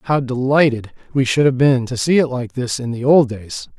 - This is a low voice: Yes, low, 130 Hz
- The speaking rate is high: Yes, fast, 240 wpm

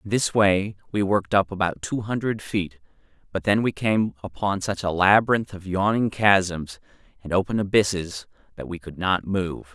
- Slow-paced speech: No, average, 180 wpm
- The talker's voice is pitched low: Yes, very low, 95 Hz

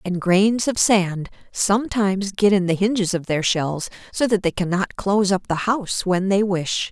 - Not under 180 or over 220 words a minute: Yes, average, 200 wpm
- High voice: Yes, high, 195 Hz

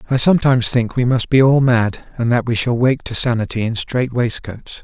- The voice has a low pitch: Yes, low, 120 Hz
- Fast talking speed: Yes, fast, 225 wpm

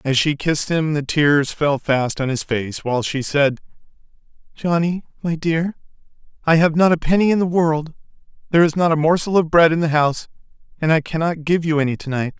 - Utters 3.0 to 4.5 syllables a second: No, 5.5 syllables/s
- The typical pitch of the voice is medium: Yes, medium, 155 Hz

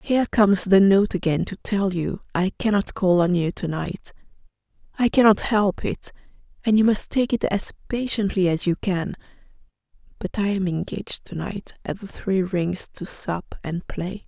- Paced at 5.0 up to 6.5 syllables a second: No, 4.7 syllables/s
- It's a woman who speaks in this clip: Yes, female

